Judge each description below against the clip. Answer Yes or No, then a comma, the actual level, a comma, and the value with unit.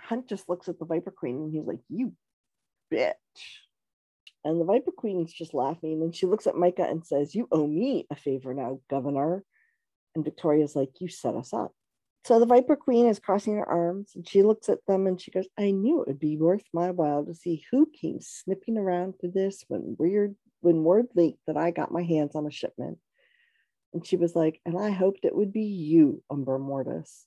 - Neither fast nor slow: No, fast, 215 wpm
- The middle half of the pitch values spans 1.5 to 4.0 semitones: No, average, 4.6 semitones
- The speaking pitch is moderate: Yes, medium, 175 Hz